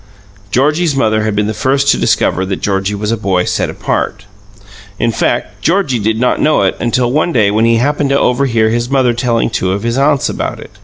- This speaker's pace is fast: Yes, fast, 215 wpm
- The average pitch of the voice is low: Yes, low, 115 Hz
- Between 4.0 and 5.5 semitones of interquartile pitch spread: Yes, average, 4.4 semitones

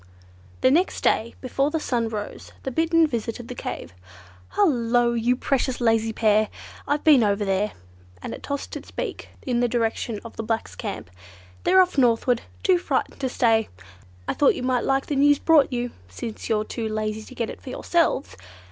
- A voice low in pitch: No, high, 240 Hz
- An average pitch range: Yes, average, 3.6 semitones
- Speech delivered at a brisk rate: No, average, 185 wpm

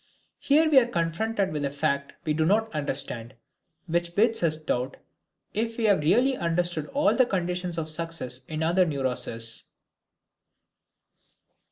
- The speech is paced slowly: No, average, 145 wpm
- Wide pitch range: Yes, wide, 5.8 semitones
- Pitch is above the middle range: No, medium, 165 Hz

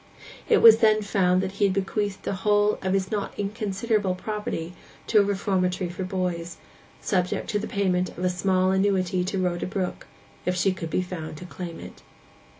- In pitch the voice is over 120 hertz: Yes, high, 190 Hz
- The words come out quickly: No, average, 185 wpm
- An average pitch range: No, narrow, 2.0 semitones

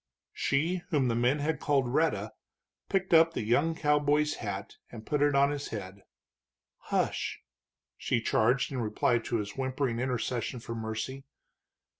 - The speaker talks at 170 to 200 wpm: No, average, 150 wpm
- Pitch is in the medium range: No, low, 130 Hz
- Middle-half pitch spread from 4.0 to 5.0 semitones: Yes, average, 4.3 semitones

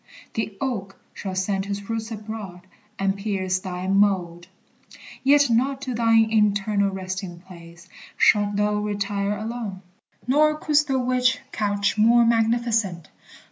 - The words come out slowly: Yes, slow, 130 wpm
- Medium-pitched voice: No, high, 205 Hz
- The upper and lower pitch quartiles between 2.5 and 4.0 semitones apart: Yes, average, 3.1 semitones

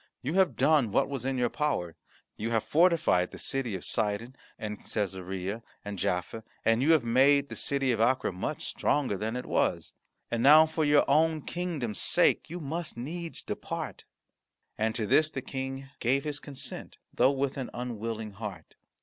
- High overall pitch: No, low, 130 Hz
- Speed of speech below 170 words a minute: No, average, 175 wpm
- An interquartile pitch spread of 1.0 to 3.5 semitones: No, average, 5.1 semitones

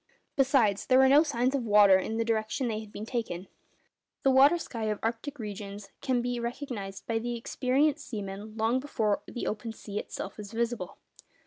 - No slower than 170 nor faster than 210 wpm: Yes, average, 185 wpm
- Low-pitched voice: No, high, 230 Hz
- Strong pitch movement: No, average, 3.7 semitones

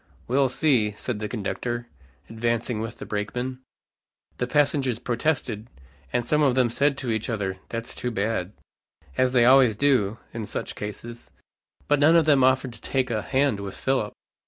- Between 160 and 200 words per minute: Yes, average, 170 wpm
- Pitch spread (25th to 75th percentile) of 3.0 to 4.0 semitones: Yes, average, 3.4 semitones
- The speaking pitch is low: Yes, low, 120 Hz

